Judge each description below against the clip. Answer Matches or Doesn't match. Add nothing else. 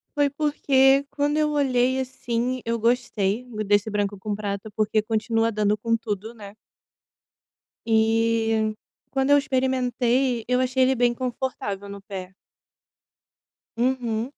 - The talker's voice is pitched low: Doesn't match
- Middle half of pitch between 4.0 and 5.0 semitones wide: Doesn't match